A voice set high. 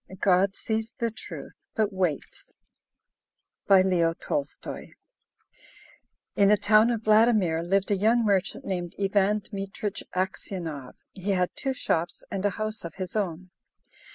Yes: high, 195 Hz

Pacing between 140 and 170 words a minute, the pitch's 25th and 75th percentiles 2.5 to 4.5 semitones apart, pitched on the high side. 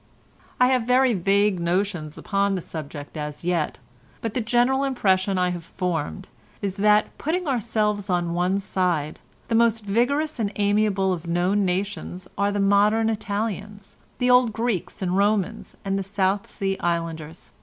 Yes: average, 155 wpm; average, 3.5 semitones; high, 200 Hz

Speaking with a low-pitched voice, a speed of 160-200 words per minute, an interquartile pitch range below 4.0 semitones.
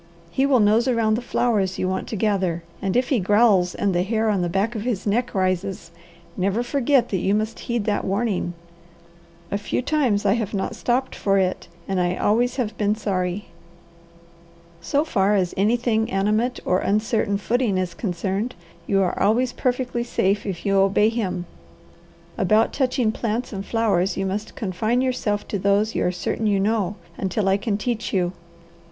No: high, 210 Hz; average, 180 wpm; average, 3.3 semitones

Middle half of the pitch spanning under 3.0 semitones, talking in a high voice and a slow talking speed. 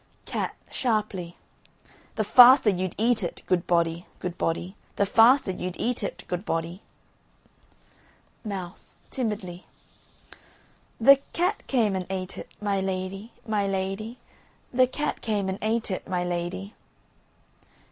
No: average, 3.6 semitones; high, 195 Hz; slow, 125 wpm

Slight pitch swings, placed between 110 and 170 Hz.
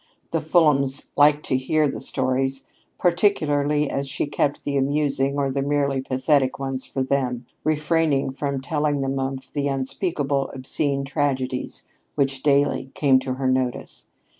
Yes: narrow, 1.7 semitones; medium, 140 Hz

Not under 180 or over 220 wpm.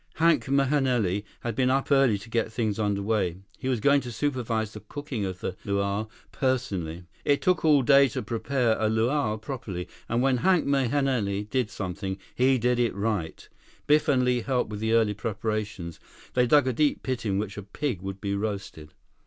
Yes: average, 190 wpm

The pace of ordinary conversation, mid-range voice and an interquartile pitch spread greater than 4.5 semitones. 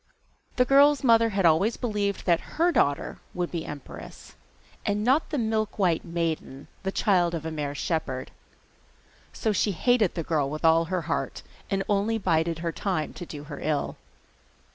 Yes: average, 165 wpm; medium, 180 Hz; average, 5.2 semitones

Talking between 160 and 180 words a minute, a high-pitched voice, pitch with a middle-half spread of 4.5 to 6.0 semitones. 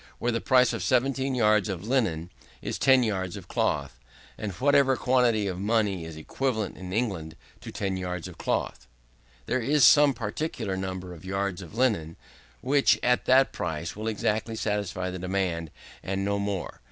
No: average, 170 wpm; low, 105 Hz; average, 5.1 semitones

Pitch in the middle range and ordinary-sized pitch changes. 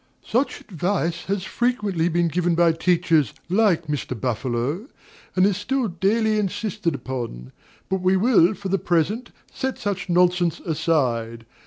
Yes: medium, 175 Hz; average, 4.2 semitones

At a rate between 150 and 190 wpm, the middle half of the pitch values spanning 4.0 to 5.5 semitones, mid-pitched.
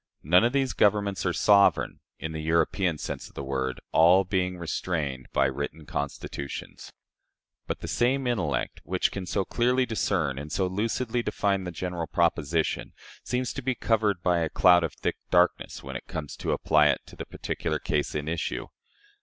No: average, 180 wpm; average, 4.8 semitones; very low, 90 Hz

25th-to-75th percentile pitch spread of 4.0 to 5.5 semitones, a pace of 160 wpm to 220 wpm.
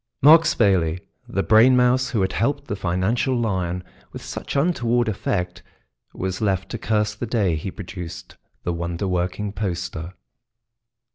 No: average, 4.8 semitones; average, 145 wpm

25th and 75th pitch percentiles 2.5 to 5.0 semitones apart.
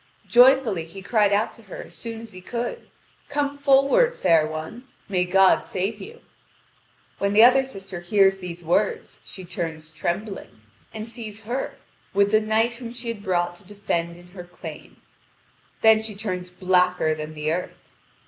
Yes: average, 4.4 semitones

